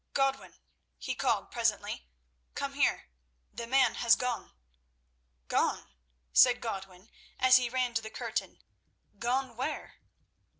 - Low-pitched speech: No, high, 240 Hz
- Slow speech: Yes, slow, 120 wpm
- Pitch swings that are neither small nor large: No, narrow, 2.3 semitones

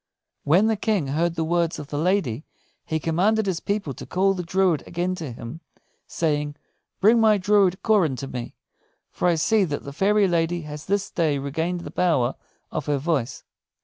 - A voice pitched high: No, medium, 170 Hz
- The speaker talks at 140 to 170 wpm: No, average, 185 wpm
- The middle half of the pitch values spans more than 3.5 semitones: Yes, average, 4.6 semitones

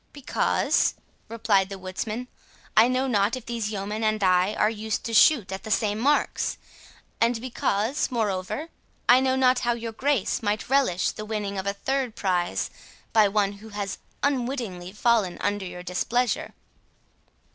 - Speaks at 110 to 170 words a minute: Yes, average, 155 wpm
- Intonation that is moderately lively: Yes, average, 3.5 semitones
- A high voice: Yes, high, 215 Hz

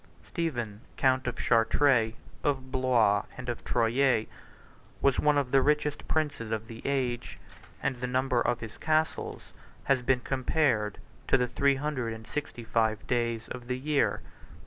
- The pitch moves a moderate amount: Yes, average, 3.2 semitones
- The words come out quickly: No, average, 155 wpm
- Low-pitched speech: Yes, low, 125 Hz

